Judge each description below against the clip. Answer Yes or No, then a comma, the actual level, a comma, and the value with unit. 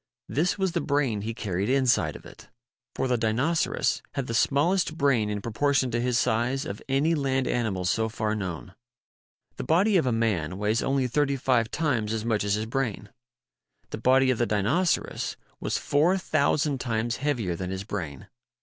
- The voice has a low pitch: Yes, low, 120 Hz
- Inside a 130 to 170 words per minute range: No, average, 185 wpm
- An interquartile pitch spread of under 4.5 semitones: No, average, 4.8 semitones